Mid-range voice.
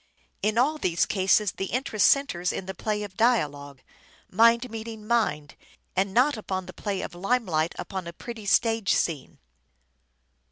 No: high, 205 Hz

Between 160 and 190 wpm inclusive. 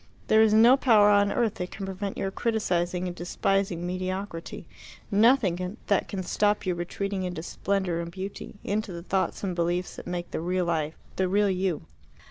Yes: average, 180 wpm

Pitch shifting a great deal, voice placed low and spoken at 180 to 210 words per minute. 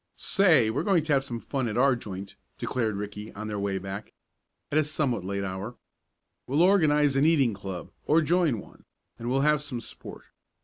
Yes: wide, 6.4 semitones; low, 125 Hz; average, 190 wpm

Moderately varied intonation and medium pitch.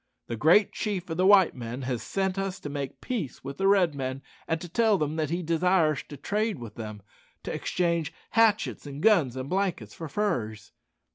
No: wide, 6.3 semitones; medium, 160 Hz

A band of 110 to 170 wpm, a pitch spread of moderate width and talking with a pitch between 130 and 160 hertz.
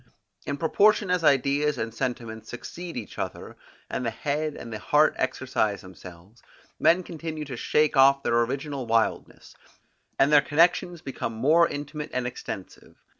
Yes: average, 150 wpm; average, 4.8 semitones; medium, 140 Hz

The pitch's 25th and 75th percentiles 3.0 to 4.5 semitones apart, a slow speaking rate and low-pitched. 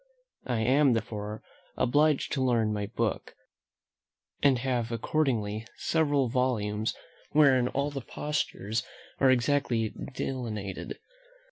Yes: average, 3.8 semitones; slow, 105 wpm; low, 125 Hz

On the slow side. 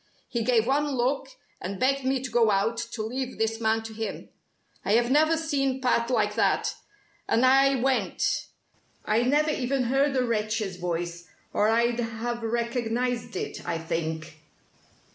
No: average, 160 wpm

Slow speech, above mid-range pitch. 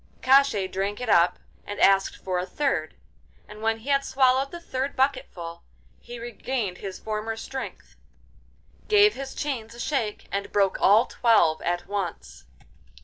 No: average, 150 wpm; high, 225 Hz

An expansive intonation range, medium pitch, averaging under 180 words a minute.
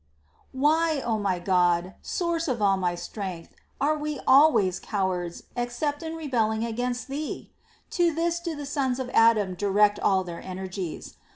No: wide, 7.7 semitones; high, 230 Hz; average, 155 wpm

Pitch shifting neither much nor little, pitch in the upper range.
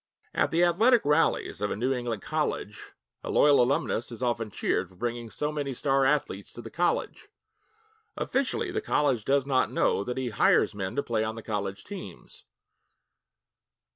No: average, 4.9 semitones; low, 125 Hz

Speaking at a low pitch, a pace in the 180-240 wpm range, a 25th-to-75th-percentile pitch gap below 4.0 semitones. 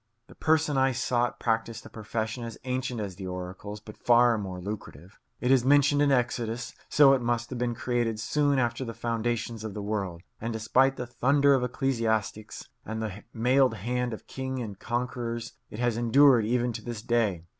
Yes: low, 120 Hz; average, 190 wpm; narrow, 2.6 semitones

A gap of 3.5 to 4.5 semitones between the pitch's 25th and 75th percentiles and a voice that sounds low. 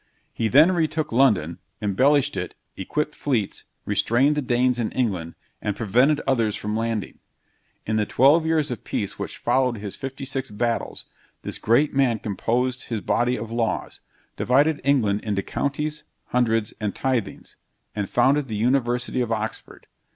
Yes: average, 3.9 semitones; low, 120 Hz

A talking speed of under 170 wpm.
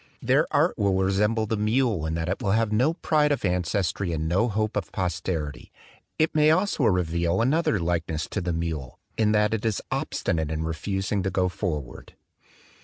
No: average, 180 wpm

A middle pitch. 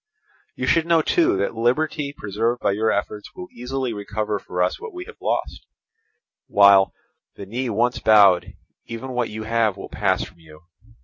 No: low, 110 Hz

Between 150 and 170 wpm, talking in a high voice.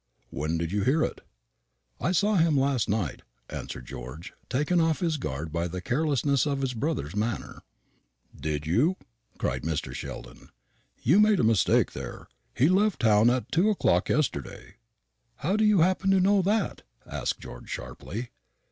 No: average, 160 wpm; low, 135 Hz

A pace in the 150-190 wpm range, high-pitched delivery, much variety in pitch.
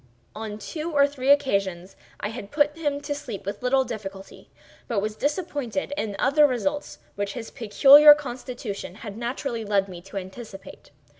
Yes: average, 160 wpm; high, 240 Hz; wide, 6.1 semitones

